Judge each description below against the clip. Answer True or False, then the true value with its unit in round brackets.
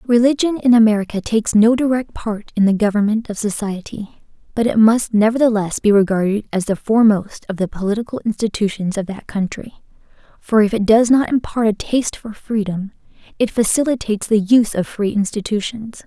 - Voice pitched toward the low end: False (215 Hz)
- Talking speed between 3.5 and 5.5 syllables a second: False (5.7 syllables/s)